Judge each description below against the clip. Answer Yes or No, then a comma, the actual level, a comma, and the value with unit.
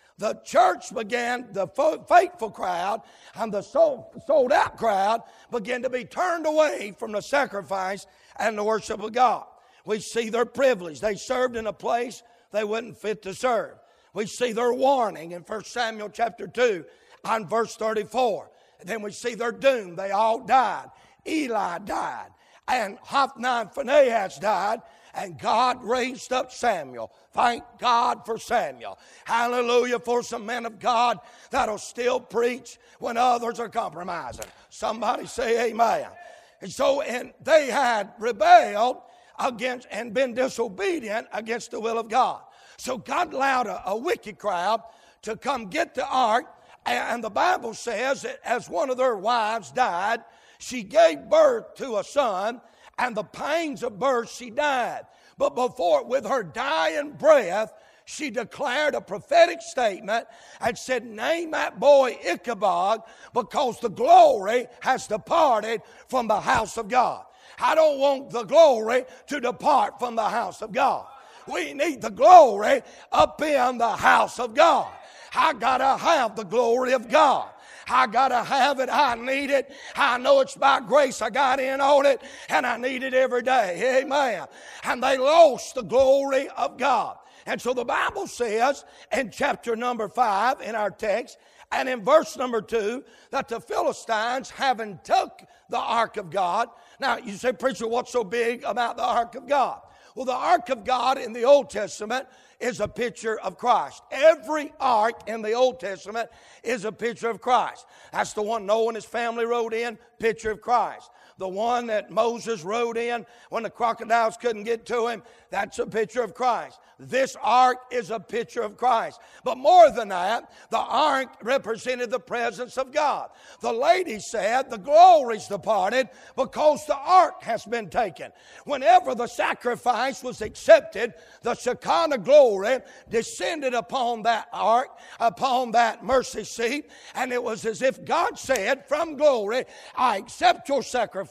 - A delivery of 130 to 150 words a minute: No, average, 165 wpm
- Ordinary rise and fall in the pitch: Yes, average, 3.2 semitones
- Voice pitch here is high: Yes, high, 245 Hz